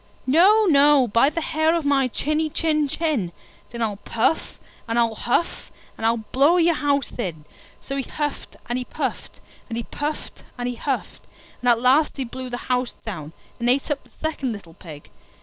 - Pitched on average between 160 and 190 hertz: No, very high, 260 Hz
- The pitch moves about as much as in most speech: Yes, average, 4.5 semitones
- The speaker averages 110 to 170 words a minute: No, average, 190 wpm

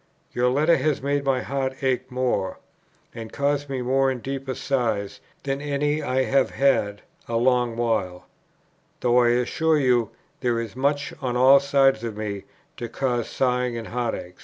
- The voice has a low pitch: Yes, low, 130 Hz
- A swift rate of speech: No, average, 165 wpm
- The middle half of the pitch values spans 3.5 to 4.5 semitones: No, average, 2.7 semitones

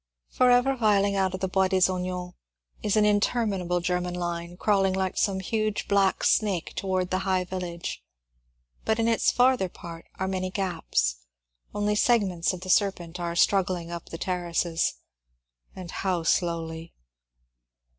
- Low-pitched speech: No, medium, 185 Hz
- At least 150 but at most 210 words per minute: Yes, average, 155 wpm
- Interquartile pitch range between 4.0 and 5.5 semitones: No, narrow, 2.4 semitones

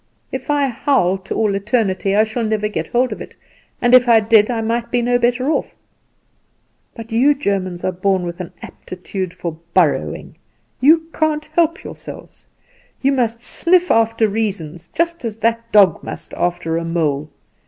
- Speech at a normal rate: Yes, average, 170 wpm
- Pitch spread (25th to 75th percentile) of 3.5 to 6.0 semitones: Yes, average, 5.0 semitones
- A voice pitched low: No, high, 225 Hz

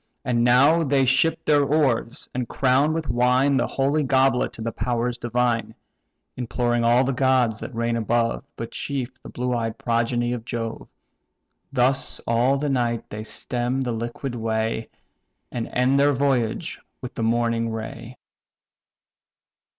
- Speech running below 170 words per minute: Yes, average, 150 wpm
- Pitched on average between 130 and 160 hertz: No, low, 120 Hz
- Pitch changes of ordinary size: No, narrow, 2.3 semitones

